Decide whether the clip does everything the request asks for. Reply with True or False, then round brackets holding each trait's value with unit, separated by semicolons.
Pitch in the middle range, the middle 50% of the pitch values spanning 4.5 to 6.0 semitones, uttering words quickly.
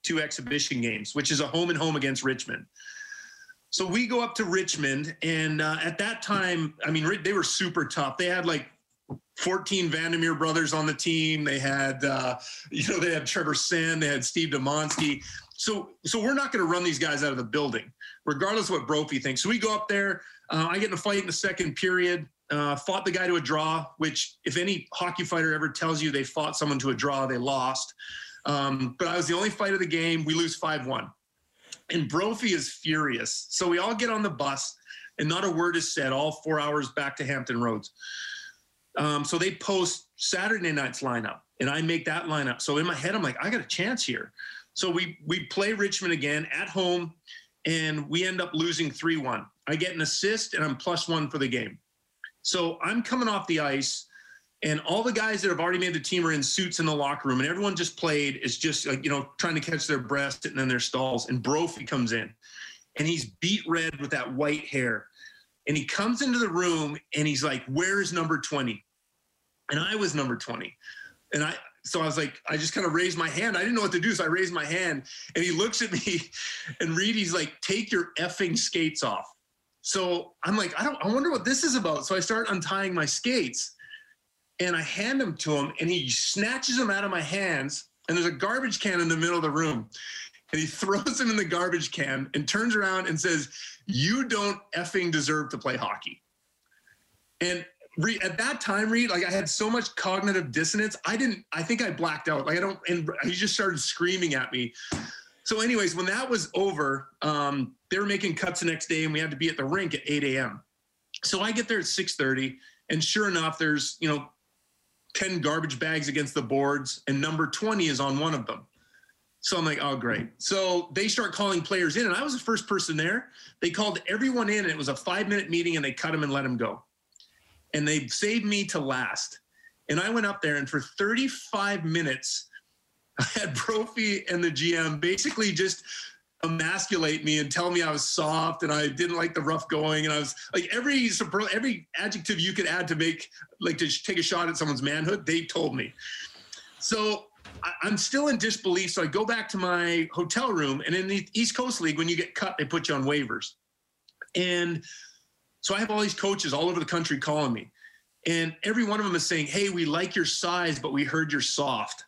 True (170 Hz; 4.8 semitones; 220 wpm)